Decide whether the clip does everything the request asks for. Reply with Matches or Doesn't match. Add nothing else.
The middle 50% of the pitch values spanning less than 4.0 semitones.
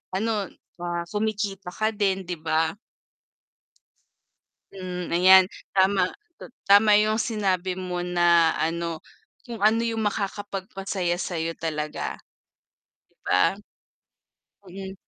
Matches